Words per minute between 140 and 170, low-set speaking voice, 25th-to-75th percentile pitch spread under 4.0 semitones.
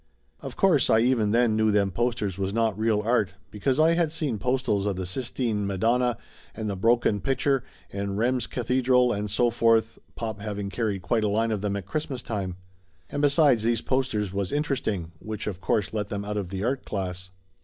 No: fast, 205 wpm; low, 110 Hz; average, 3.6 semitones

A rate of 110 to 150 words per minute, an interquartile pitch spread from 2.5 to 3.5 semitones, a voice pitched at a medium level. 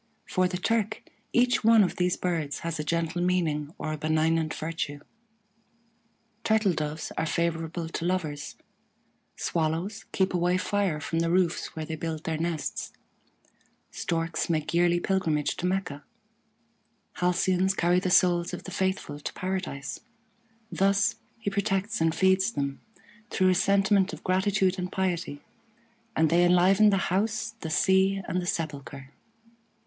Yes: average, 145 wpm; average, 2.9 semitones; medium, 175 Hz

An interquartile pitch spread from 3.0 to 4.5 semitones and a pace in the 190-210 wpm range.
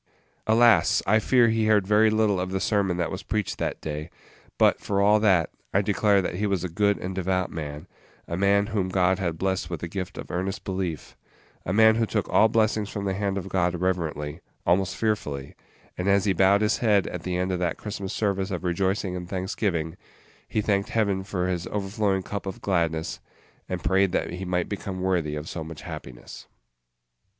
No: narrow, 2.4 semitones; average, 200 wpm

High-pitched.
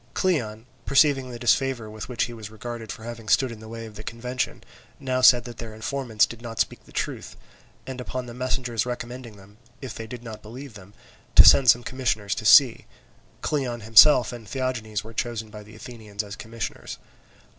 No: low, 115 Hz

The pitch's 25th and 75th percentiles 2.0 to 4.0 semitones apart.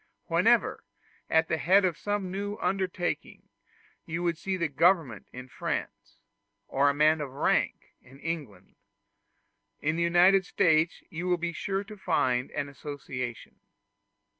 No: average, 4.4 semitones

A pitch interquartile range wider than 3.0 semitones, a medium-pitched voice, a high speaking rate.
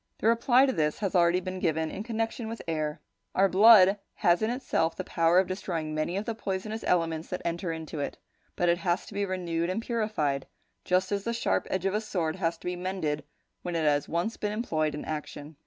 Yes: average, 4.3 semitones; medium, 180 Hz; fast, 220 wpm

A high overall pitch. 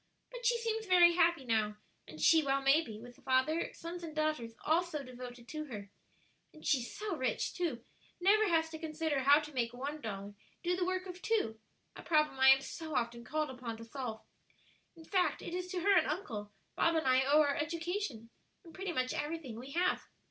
Yes: very high, 305 Hz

